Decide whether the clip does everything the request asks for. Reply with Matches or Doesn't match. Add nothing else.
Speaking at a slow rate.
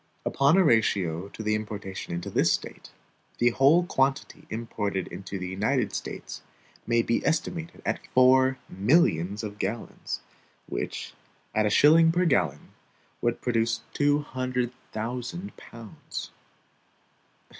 Matches